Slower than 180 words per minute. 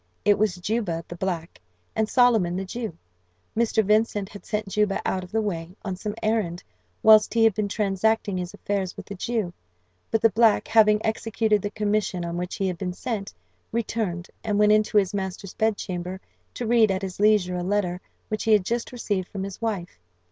No: average, 195 wpm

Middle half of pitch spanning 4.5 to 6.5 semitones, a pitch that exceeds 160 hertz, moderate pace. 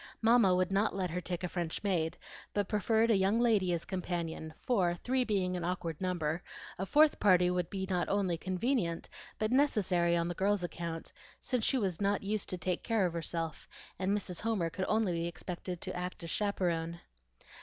No: average, 3.1 semitones; medium, 185 Hz; average, 195 wpm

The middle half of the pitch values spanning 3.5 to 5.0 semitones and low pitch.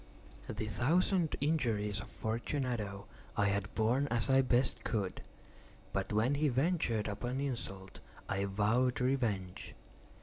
Yes: average, 4.6 semitones; low, 120 Hz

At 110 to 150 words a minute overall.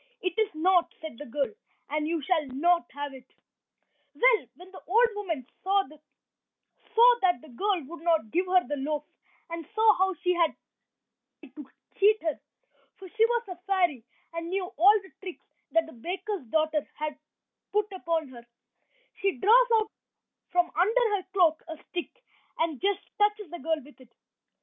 No: average, 170 wpm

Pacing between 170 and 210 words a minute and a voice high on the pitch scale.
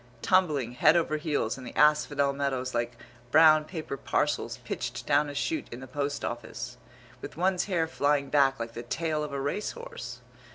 No: average, 180 wpm; medium, 145 Hz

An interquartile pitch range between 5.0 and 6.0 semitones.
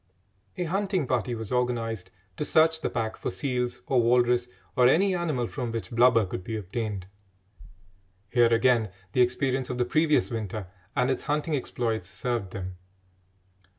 No: average, 2.8 semitones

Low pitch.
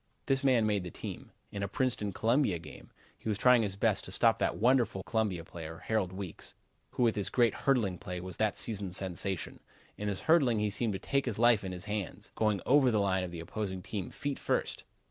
Yes: low, 105 Hz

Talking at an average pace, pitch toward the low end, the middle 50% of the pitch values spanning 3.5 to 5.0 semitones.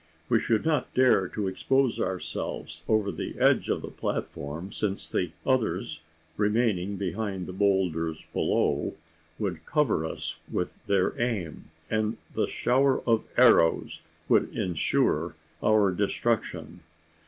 No: slow, 125 wpm; low, 100 Hz; average, 4.1 semitones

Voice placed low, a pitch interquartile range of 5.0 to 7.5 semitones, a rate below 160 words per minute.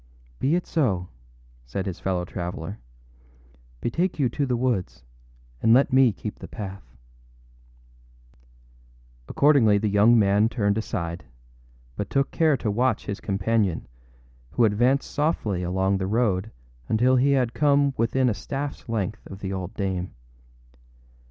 Yes: low, 105 Hz; wide, 5.5 semitones; average, 140 wpm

